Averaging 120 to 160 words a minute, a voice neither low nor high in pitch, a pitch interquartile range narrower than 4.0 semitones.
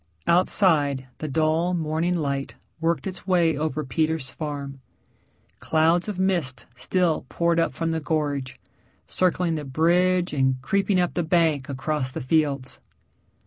Yes: average, 140 wpm; medium, 160 Hz; average, 3.5 semitones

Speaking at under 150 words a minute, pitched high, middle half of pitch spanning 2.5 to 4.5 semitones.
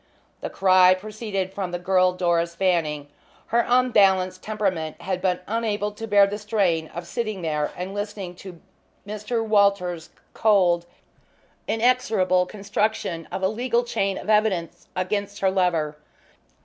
Yes: slow, 135 wpm; high, 195 Hz; average, 2.9 semitones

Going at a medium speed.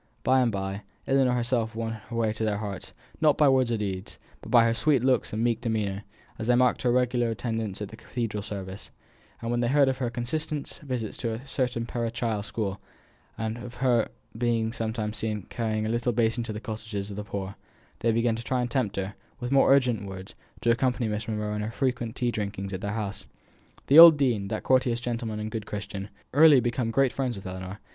No: fast, 220 wpm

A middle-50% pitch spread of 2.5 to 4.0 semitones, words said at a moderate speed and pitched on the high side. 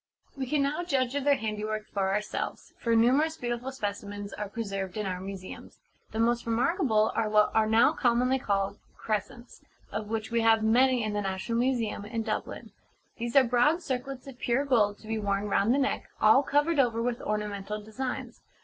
Yes: average, 3.5 semitones; average, 185 wpm; high, 225 Hz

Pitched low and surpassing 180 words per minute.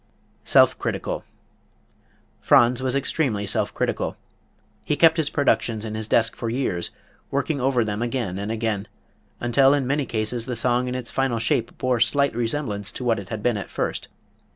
No: low, 120 Hz; average, 175 wpm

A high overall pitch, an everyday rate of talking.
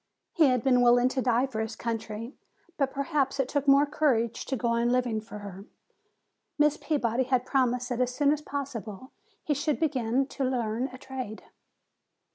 Yes: very high, 255 Hz; average, 180 wpm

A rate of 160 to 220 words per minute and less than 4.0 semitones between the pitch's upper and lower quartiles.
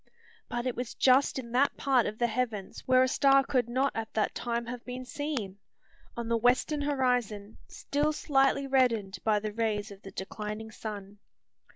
Yes: average, 180 wpm; average, 3.6 semitones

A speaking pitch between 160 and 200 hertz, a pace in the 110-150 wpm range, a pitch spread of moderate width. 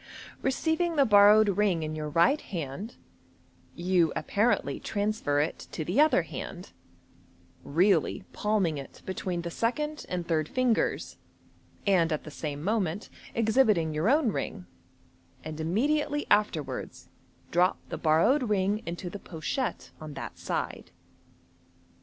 No: high, 190 Hz; slow, 135 wpm; wide, 5.7 semitones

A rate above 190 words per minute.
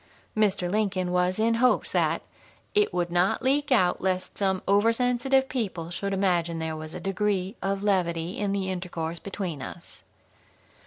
No: average, 155 wpm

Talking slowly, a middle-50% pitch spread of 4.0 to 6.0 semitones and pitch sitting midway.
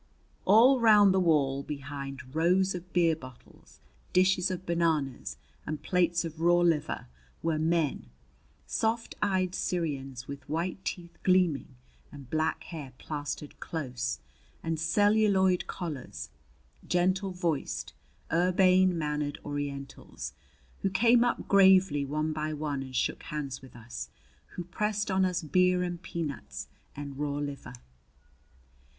Yes: slow, 125 wpm; average, 4.5 semitones; medium, 165 Hz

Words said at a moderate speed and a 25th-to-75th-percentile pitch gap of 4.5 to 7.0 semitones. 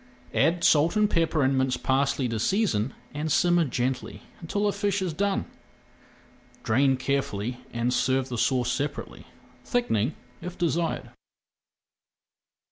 No: slow, 125 wpm; wide, 5.6 semitones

